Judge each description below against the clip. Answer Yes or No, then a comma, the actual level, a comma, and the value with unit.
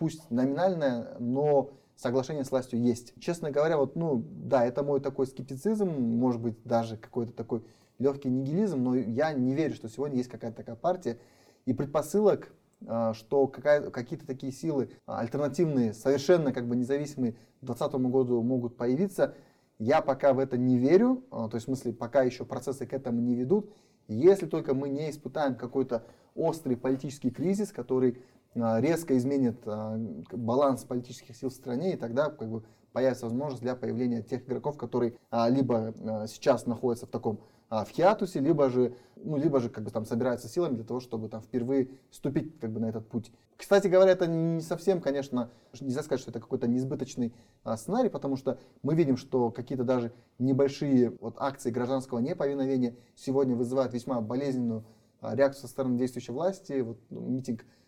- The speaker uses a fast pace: Yes, fast, 170 wpm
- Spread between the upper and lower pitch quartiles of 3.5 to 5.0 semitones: No, average, 2.7 semitones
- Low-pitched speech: Yes, low, 125 Hz